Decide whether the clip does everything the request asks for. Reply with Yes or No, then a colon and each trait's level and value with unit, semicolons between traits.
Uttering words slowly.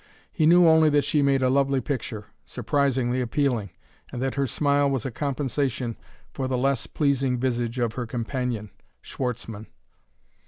No: average, 155 wpm